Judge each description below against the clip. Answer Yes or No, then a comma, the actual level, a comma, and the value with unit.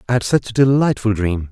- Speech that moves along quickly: Yes, fast, 240 wpm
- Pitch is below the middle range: Yes, low, 115 Hz